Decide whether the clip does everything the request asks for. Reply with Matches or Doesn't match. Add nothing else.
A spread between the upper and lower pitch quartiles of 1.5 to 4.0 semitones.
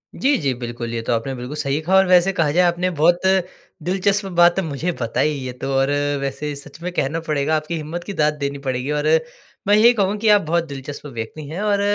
Doesn't match